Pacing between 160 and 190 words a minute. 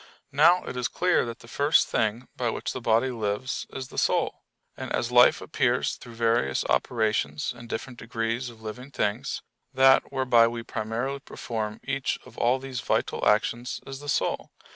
Yes: average, 175 wpm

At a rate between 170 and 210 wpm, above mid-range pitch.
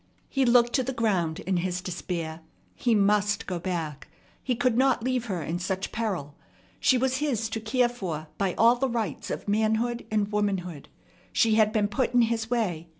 Yes: average, 190 wpm; high, 215 Hz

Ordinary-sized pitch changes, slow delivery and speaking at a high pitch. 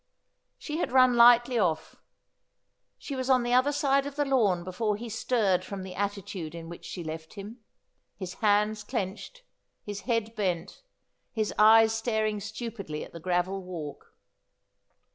No: average, 4.6 semitones; average, 155 wpm; high, 210 Hz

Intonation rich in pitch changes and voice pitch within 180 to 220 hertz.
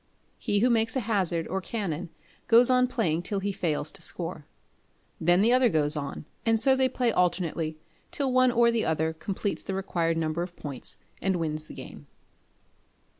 Yes: wide, 6.1 semitones; high, 190 Hz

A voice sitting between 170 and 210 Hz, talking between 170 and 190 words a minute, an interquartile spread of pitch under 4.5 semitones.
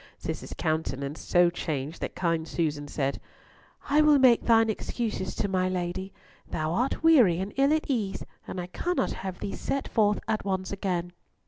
No: high, 190 Hz; average, 175 wpm; average, 5.3 semitones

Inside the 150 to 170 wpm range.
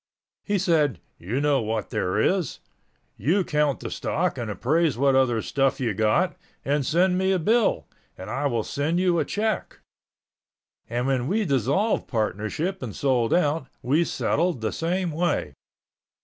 Yes: average, 160 wpm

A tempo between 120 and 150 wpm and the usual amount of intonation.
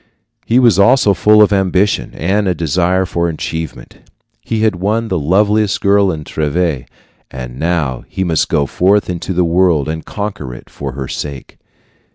No: average, 170 wpm; average, 4.6 semitones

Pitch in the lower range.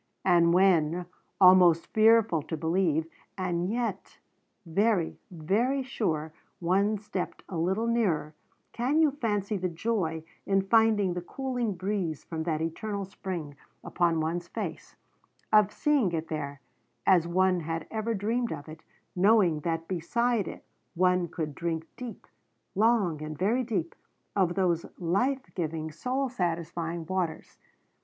No: medium, 185 Hz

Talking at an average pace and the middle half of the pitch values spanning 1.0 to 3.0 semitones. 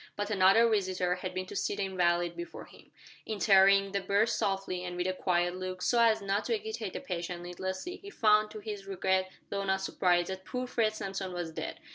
No: fast, 210 wpm; narrow, 2.5 semitones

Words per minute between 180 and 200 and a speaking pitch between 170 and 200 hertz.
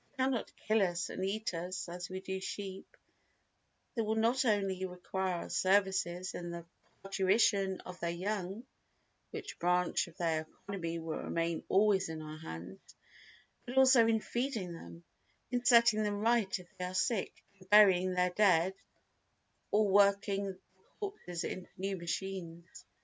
No: average, 155 wpm; high, 190 Hz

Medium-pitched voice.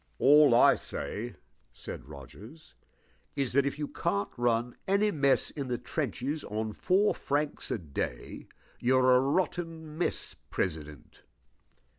No: low, 130 Hz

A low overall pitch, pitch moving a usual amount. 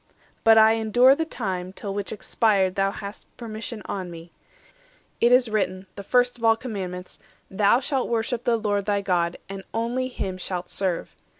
No: high, 210 Hz; average, 3.5 semitones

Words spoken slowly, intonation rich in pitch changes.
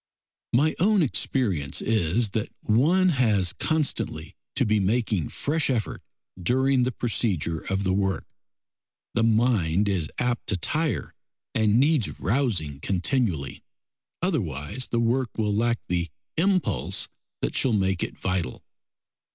Yes: slow, 125 wpm; wide, 5.8 semitones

